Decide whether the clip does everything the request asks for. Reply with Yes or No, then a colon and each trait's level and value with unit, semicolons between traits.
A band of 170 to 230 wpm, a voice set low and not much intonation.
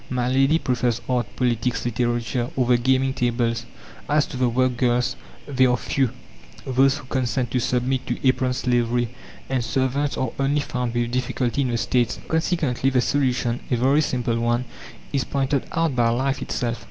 Yes: average, 175 wpm; low, 125 Hz; narrow, 1.8 semitones